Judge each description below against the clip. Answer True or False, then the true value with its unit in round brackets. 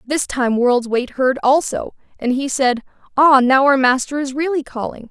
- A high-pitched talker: True (265 Hz)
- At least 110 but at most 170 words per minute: False (190 wpm)